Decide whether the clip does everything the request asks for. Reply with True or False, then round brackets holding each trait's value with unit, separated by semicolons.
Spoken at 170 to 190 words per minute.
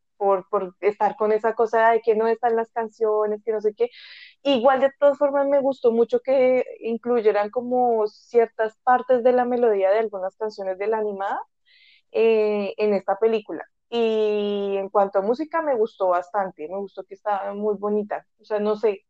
True (185 wpm)